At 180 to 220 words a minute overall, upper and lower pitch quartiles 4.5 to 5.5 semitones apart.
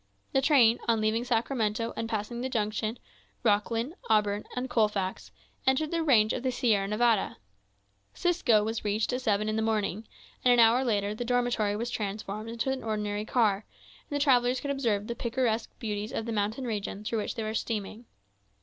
No: average, 185 wpm; narrow, 2.5 semitones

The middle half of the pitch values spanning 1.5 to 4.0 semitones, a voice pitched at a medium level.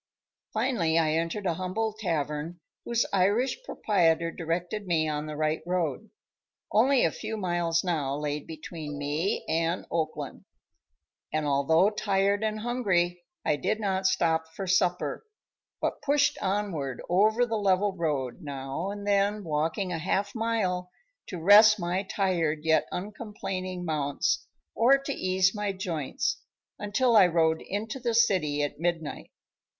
No: average, 4.5 semitones; medium, 180 Hz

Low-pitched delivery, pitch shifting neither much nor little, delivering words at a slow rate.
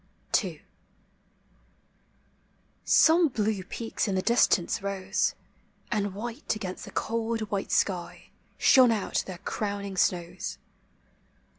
No: high, 205 Hz; average, 3.3 semitones; slow, 105 wpm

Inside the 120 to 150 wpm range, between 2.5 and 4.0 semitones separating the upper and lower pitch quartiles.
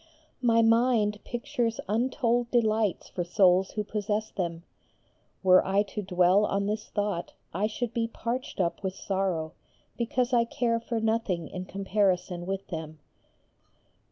Yes: average, 140 wpm; average, 3.7 semitones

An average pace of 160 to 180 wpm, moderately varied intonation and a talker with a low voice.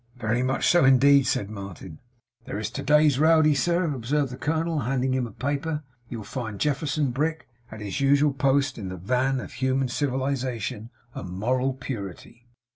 Yes: average, 170 wpm; average, 3.5 semitones; low, 130 Hz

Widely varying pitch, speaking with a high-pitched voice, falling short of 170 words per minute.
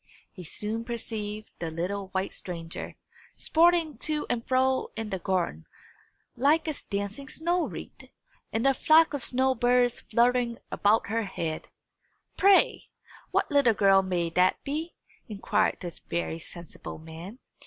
Yes: wide, 6.0 semitones; high, 225 Hz; average, 140 wpm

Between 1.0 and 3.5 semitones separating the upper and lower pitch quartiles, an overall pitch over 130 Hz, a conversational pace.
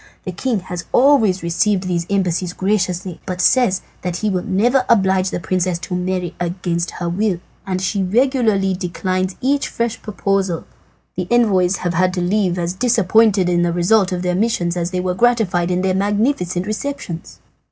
Yes: average, 3.0 semitones; medium, 185 Hz; average, 175 wpm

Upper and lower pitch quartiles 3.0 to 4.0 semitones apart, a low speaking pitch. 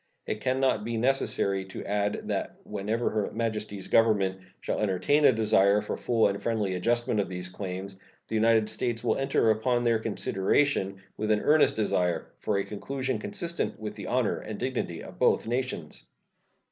Yes: average, 3.4 semitones; low, 110 Hz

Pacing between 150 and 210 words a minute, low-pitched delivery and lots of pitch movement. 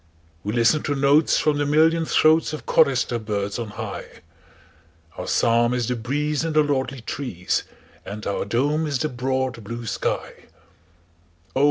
No: average, 140 wpm; low, 125 Hz; wide, 5.9 semitones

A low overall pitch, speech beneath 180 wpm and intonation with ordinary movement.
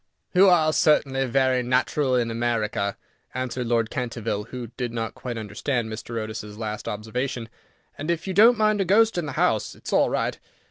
No: low, 125 Hz; average, 185 wpm; average, 4.6 semitones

